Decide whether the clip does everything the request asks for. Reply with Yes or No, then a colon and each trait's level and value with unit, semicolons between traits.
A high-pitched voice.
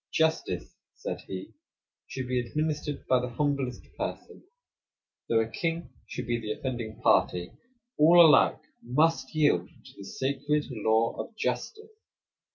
No: low, 130 Hz